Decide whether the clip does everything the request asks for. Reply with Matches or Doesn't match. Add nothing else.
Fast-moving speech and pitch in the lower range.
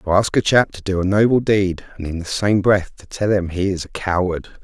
Matches